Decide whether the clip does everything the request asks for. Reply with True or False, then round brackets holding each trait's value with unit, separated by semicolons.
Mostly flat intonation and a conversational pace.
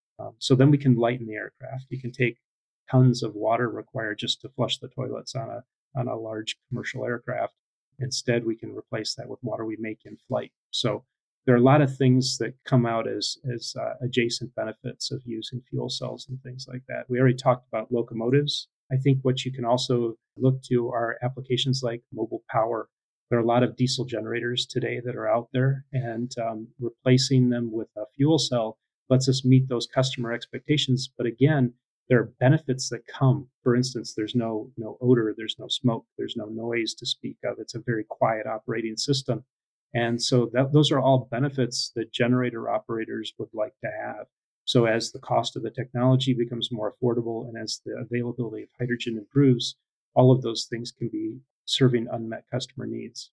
True (1.9 semitones; 195 wpm)